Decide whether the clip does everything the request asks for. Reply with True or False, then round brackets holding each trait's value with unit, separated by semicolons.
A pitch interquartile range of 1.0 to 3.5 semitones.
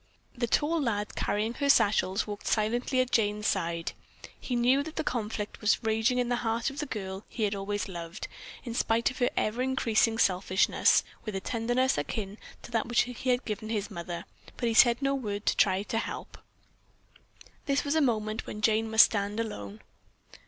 True (3.1 semitones)